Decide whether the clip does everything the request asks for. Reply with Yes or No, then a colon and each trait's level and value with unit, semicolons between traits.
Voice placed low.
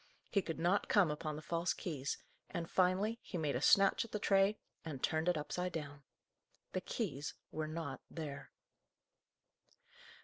No: medium, 165 Hz